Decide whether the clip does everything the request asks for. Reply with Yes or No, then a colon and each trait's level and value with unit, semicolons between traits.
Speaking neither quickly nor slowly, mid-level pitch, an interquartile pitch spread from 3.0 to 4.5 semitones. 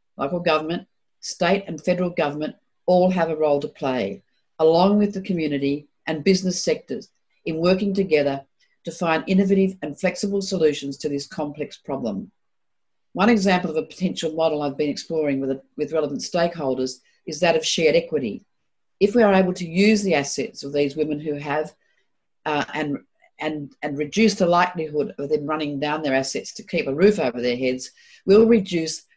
Yes: average, 175 wpm; medium, 160 Hz; average, 4.0 semitones